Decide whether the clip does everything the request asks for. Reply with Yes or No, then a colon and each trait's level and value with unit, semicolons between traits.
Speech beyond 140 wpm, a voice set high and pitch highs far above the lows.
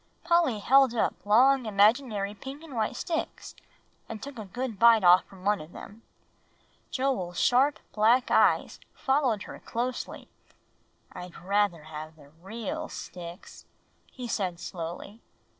No: slow, 135 wpm; high, 220 Hz; wide, 5.8 semitones